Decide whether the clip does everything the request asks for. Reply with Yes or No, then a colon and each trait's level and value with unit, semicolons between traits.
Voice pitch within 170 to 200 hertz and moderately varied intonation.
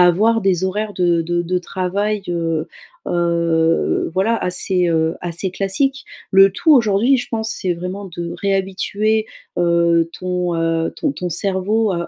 Yes: medium, 185 Hz; average, 3.1 semitones